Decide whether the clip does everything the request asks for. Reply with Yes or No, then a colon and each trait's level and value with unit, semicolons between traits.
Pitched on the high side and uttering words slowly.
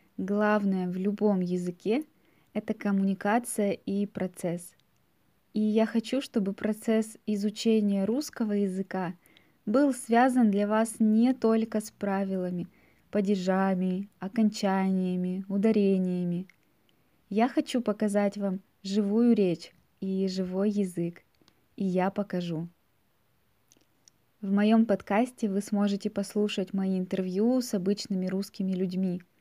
Yes: high, 200 Hz; slow, 105 wpm